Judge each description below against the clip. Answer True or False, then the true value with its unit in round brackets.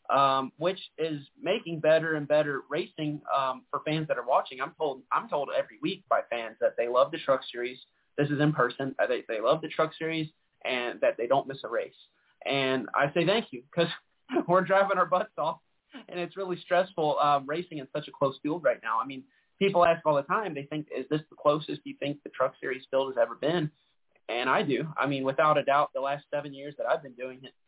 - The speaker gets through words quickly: True (235 wpm)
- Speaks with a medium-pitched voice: True (150 Hz)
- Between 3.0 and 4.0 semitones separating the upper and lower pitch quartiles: True (3.7 semitones)